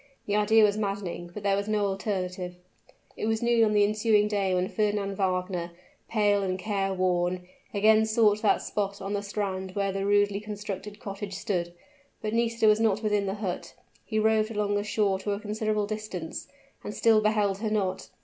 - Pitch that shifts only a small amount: Yes, narrow, 1.7 semitones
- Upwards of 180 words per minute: Yes, average, 190 wpm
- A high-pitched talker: Yes, high, 205 Hz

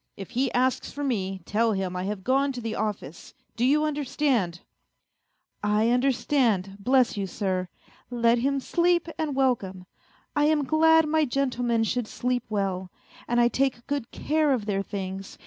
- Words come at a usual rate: Yes, average, 170 wpm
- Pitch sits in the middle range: No, high, 240 Hz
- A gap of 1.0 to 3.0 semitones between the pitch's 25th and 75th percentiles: No, wide, 5.6 semitones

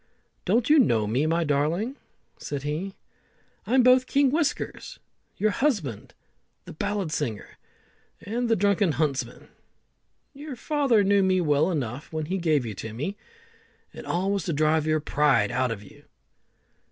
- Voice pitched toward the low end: No, medium, 170 Hz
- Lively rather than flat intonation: Yes, wide, 6.9 semitones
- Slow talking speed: No, average, 155 wpm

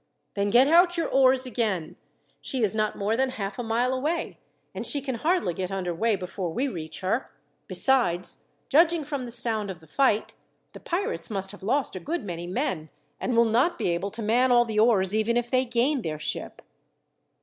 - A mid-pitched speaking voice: No, high, 230 Hz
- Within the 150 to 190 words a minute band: No, fast, 205 wpm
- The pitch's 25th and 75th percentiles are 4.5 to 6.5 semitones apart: Yes, average, 5.3 semitones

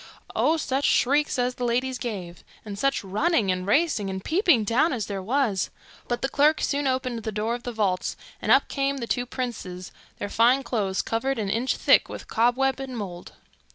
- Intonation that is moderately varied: Yes, average, 4.7 semitones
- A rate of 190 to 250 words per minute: Yes, average, 195 wpm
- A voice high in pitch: Yes, high, 240 Hz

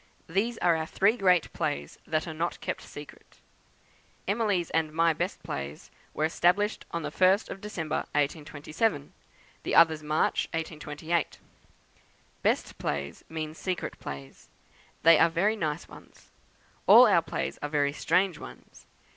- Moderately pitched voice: Yes, medium, 160 Hz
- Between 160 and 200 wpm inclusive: No, average, 140 wpm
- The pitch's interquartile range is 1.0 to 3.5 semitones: Yes, average, 3.2 semitones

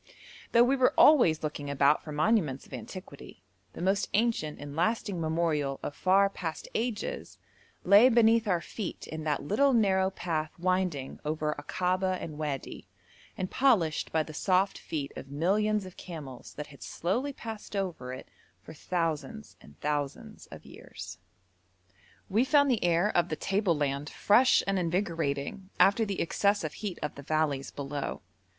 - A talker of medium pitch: Yes, medium, 175 Hz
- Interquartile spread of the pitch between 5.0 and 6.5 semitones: Yes, average, 5.3 semitones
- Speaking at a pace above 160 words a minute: No, average, 155 wpm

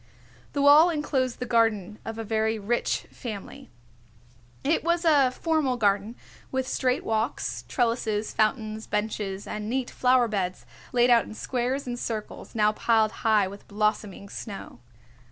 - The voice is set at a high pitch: Yes, high, 225 Hz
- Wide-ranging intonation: No, average, 3.2 semitones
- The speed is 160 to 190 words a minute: No, average, 145 wpm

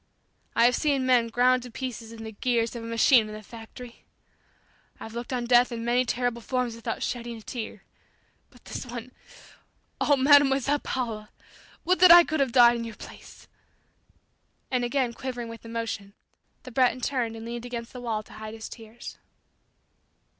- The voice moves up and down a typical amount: No, narrow, 1.9 semitones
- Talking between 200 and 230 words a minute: No, average, 175 wpm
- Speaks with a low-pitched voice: No, high, 240 Hz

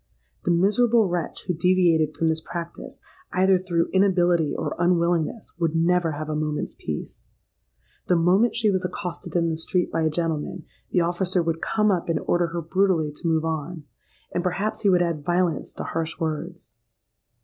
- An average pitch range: No, narrow, 2.1 semitones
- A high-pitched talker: No, medium, 175 Hz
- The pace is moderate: Yes, average, 175 wpm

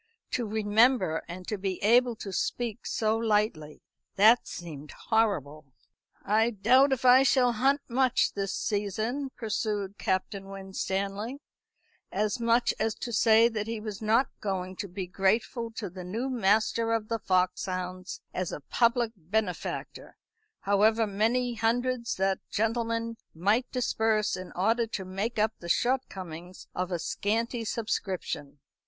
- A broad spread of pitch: No, average, 3.4 semitones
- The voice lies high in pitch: Yes, high, 215 Hz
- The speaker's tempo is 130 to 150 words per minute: Yes, average, 140 wpm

